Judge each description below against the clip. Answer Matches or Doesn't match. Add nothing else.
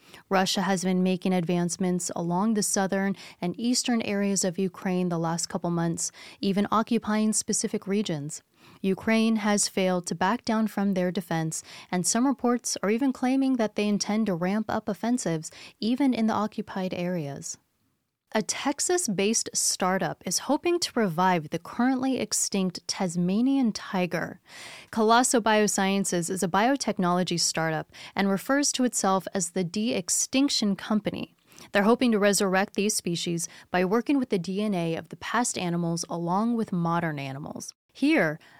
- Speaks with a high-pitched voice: Matches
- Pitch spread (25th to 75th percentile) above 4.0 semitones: Doesn't match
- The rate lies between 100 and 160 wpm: Matches